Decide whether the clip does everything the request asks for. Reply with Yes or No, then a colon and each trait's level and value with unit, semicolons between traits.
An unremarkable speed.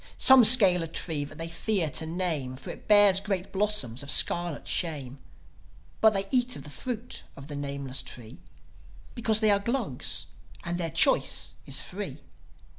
Yes: average, 170 wpm